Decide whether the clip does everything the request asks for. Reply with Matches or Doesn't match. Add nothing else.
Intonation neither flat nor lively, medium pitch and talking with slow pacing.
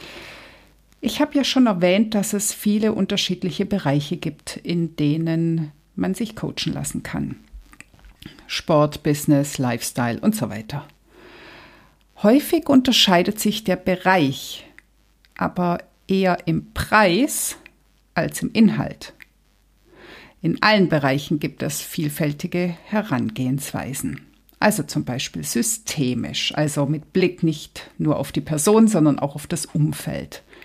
Doesn't match